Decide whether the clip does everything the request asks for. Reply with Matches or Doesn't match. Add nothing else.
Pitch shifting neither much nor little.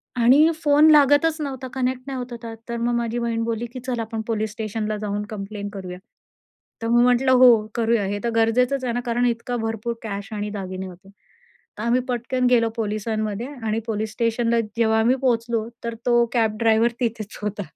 Doesn't match